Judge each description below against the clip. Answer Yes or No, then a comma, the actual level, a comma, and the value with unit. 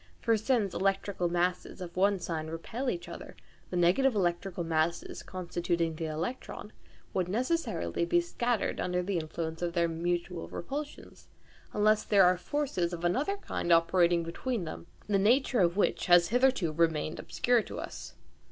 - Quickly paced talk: No, average, 155 wpm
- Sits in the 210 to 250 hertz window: No, medium, 180 Hz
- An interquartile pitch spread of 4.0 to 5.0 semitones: Yes, average, 4.7 semitones